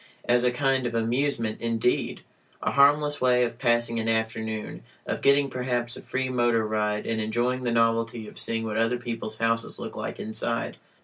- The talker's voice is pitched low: Yes, low, 115 Hz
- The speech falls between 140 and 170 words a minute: No, average, 180 wpm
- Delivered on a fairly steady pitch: Yes, narrow, 1.8 semitones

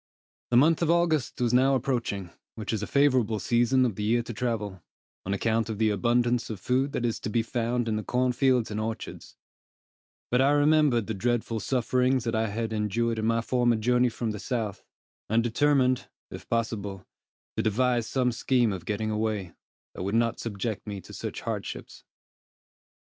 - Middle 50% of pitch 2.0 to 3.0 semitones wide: Yes, narrow, 2.5 semitones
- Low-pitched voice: Yes, low, 115 Hz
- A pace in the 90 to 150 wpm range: No, average, 185 wpm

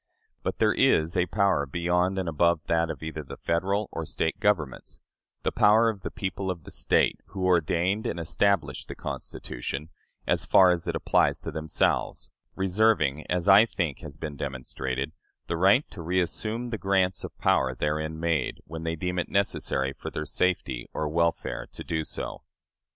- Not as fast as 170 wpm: No, average, 175 wpm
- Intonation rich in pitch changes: No, average, 3.6 semitones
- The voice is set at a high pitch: No, very low, 85 Hz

